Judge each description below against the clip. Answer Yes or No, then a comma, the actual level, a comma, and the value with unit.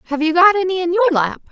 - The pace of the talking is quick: Yes, fast, 280 wpm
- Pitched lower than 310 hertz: No, very high, 345 Hz